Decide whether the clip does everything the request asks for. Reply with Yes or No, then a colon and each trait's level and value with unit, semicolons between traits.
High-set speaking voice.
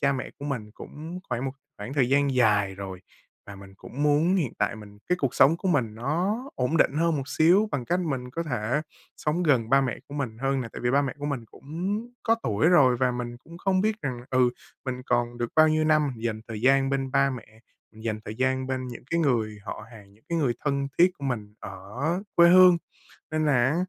No: low, 135 Hz